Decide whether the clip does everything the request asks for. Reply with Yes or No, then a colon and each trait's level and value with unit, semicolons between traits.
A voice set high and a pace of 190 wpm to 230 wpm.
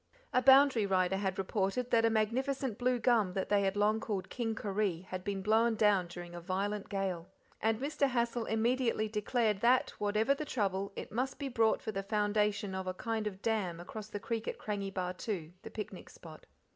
Yes: high, 210 Hz; average, 195 wpm